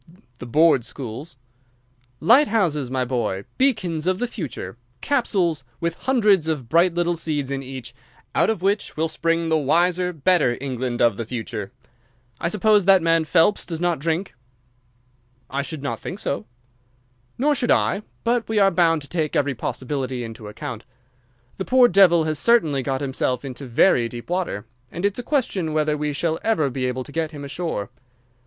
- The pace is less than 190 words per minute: Yes, average, 175 wpm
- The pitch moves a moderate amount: No, wide, 5.7 semitones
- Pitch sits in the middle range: Yes, medium, 160 Hz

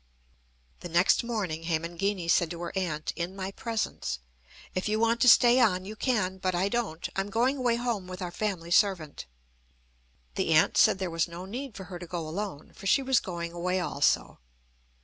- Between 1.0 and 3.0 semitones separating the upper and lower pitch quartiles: No, average, 4.0 semitones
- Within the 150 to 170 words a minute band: No, average, 190 wpm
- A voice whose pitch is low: No, medium, 185 Hz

